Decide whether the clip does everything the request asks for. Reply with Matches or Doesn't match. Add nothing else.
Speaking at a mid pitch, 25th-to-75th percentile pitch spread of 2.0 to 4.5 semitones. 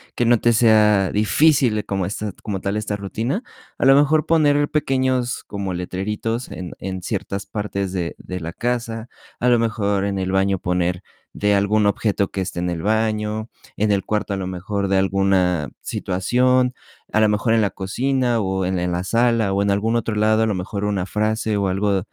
Doesn't match